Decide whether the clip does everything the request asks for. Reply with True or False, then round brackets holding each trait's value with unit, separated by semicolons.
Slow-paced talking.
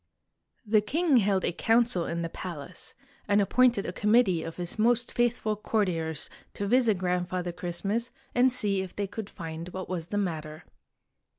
False (165 wpm)